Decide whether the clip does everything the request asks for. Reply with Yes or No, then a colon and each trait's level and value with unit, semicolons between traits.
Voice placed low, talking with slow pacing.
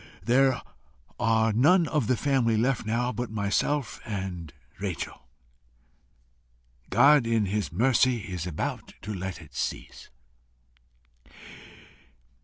Yes: low, 110 Hz; slow, 105 wpm